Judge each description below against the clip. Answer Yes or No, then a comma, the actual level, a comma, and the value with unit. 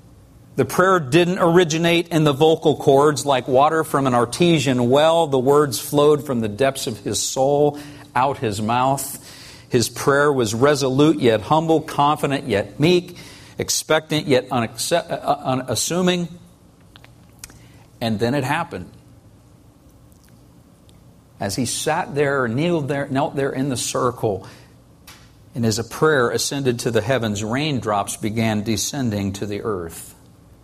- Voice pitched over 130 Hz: Yes, medium, 140 Hz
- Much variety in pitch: No, average, 4.3 semitones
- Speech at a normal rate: No, slow, 130 wpm